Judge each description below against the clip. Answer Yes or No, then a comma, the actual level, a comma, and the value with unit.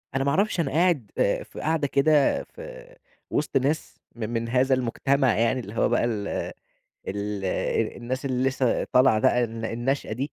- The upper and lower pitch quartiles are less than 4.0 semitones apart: Yes, average, 3.4 semitones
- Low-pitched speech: Yes, low, 130 Hz